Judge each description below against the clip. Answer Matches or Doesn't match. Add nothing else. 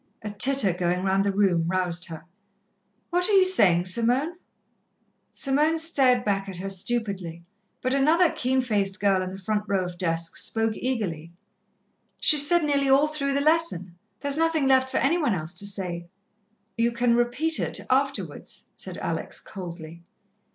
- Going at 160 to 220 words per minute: Matches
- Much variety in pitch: Matches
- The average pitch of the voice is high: Matches